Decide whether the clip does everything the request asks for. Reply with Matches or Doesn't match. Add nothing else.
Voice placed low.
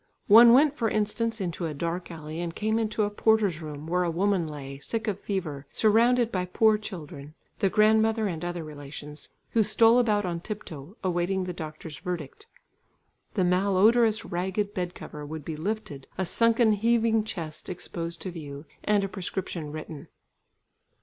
Doesn't match